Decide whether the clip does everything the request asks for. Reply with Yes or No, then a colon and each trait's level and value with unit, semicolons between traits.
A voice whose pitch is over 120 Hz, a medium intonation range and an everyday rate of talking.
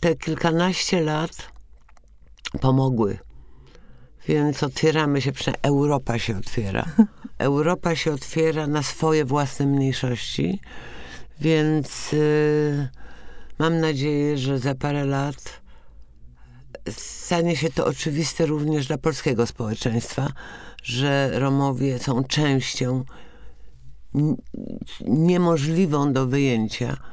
No: medium, 140 Hz; average, 3.9 semitones; slow, 95 wpm